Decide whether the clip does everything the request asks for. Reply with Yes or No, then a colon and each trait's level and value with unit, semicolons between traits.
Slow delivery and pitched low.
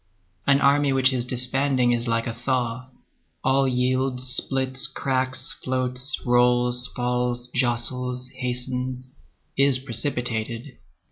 Yes: slow, 110 wpm; low, 125 Hz